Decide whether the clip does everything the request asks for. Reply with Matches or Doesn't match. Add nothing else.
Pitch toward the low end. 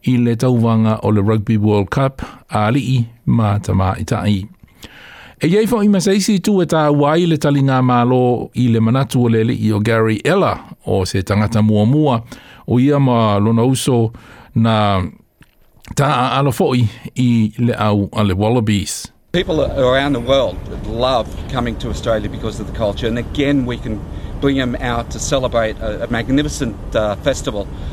Matches